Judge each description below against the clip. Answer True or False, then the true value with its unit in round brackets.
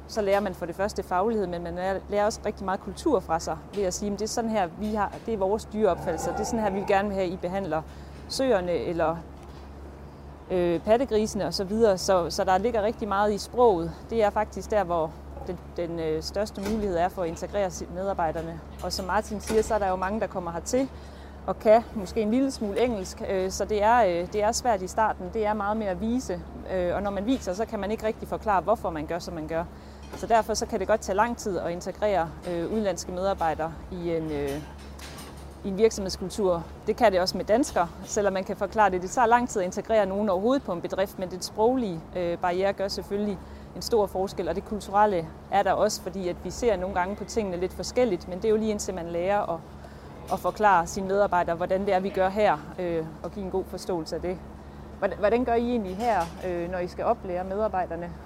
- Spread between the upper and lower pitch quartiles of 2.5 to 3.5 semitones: True (3.2 semitones)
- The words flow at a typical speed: False (235 wpm)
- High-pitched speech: True (195 Hz)